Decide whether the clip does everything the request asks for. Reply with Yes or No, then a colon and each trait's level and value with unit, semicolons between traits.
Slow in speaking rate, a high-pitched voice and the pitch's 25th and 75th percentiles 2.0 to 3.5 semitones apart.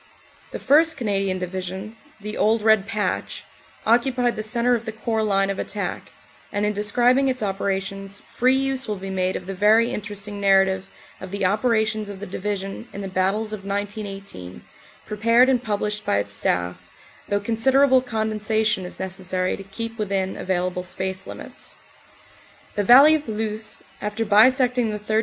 No: average, 170 wpm; high, 210 Hz; average, 2.8 semitones